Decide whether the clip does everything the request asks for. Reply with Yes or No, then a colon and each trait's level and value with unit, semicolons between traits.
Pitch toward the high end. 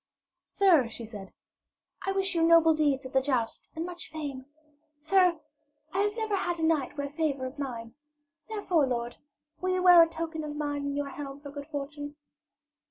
Yes: very high, 295 Hz